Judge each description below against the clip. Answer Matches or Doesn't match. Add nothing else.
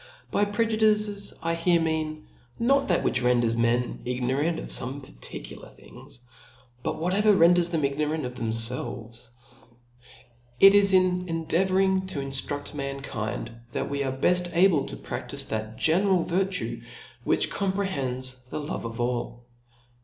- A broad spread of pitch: Matches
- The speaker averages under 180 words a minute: Matches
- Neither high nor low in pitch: Matches